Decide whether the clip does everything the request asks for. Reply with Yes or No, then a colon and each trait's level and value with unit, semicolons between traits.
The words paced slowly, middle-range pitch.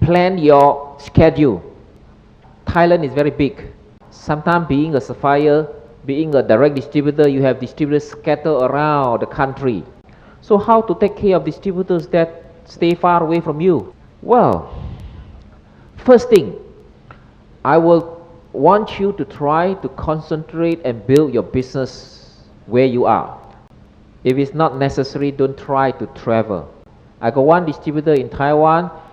Yes: slow, 140 wpm; medium, 150 Hz